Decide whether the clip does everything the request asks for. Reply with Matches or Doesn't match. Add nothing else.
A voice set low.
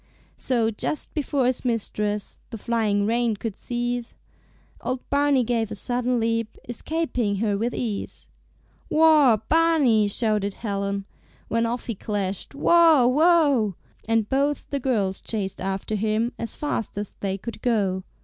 Doesn't match